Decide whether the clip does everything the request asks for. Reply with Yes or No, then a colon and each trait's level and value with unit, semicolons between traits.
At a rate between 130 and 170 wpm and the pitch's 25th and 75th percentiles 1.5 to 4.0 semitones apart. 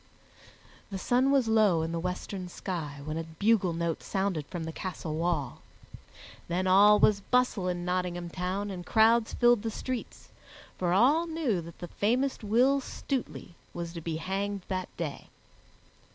No: average, 160 wpm; average, 4.6 semitones